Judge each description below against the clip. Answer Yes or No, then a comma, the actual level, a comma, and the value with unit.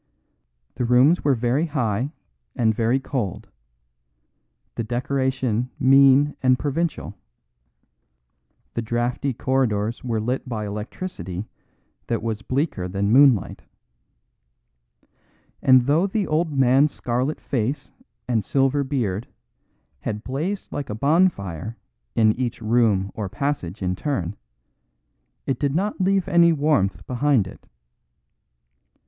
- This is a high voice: No, low, 125 Hz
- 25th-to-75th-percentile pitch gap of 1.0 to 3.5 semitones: No, average, 4.6 semitones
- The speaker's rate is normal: No, slow, 115 wpm